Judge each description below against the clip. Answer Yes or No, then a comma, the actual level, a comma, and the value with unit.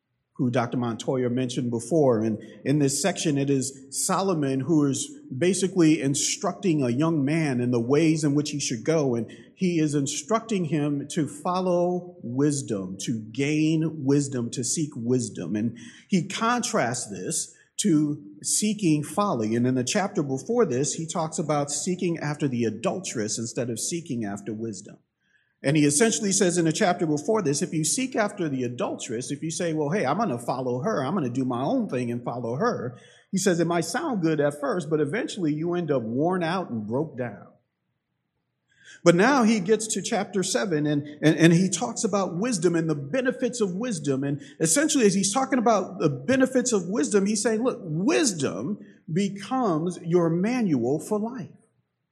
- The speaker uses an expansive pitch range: Yes, wide, 5.7 semitones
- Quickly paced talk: No, average, 180 wpm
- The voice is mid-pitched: Yes, medium, 155 Hz